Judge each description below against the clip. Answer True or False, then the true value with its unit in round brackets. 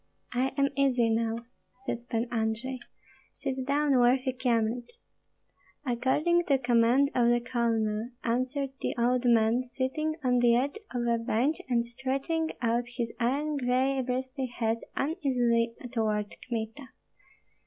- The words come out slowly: True (130 wpm)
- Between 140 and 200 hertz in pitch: False (245 Hz)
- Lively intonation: False (2.4 semitones)